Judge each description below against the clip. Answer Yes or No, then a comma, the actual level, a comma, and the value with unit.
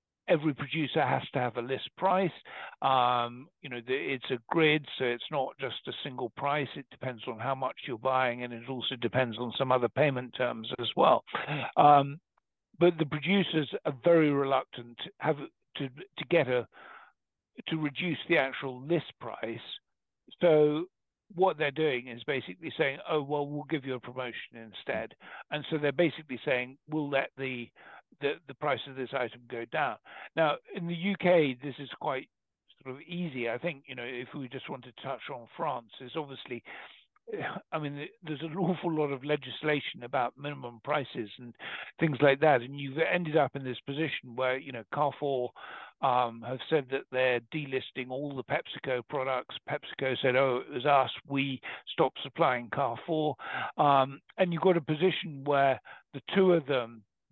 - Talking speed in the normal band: Yes, average, 180 wpm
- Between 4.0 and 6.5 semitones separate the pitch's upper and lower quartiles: No, average, 3.5 semitones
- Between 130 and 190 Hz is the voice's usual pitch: Yes, medium, 140 Hz